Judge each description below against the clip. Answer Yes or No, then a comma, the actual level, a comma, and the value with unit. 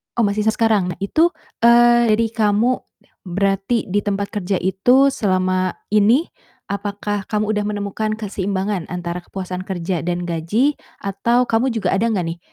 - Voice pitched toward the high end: Yes, high, 205 Hz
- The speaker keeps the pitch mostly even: No, average, 3.2 semitones